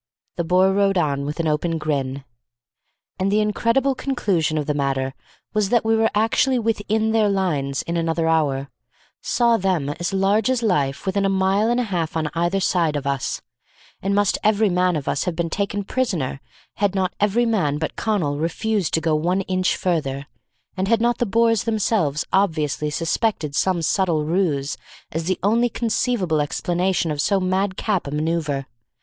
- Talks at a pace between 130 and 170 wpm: No, average, 180 wpm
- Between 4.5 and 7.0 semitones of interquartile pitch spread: Yes, average, 5.3 semitones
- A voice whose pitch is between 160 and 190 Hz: Yes, medium, 185 Hz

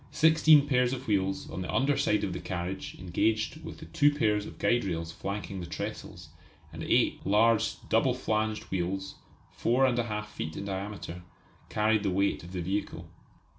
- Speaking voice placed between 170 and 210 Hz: No, low, 105 Hz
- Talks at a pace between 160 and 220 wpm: Yes, average, 170 wpm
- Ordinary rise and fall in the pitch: Yes, average, 4.1 semitones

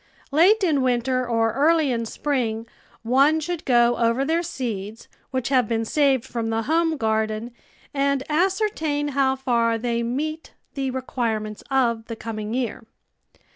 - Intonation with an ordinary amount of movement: Yes, average, 4.2 semitones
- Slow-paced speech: No, average, 145 wpm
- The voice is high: Yes, very high, 255 Hz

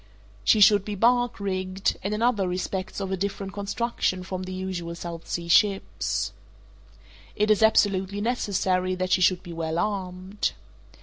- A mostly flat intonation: Yes, narrow, 1.9 semitones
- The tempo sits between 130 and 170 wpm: Yes, average, 160 wpm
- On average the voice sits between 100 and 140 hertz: No, high, 190 Hz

